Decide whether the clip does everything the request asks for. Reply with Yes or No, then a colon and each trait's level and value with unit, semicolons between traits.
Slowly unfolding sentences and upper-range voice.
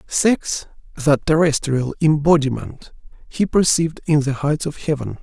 No: slow, 125 wpm; medium, 150 Hz